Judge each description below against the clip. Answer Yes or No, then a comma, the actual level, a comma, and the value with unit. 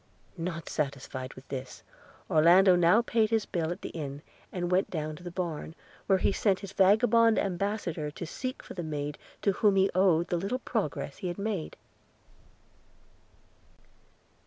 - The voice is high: No, medium, 180 Hz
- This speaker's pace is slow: No, average, 160 wpm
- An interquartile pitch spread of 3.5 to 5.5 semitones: Yes, average, 4.1 semitones